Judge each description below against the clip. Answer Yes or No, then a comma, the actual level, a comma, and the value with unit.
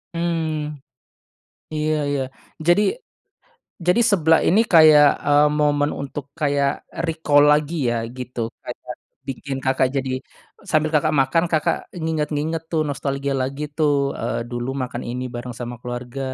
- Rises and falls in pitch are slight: No, average, 3.0 semitones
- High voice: No, medium, 145 Hz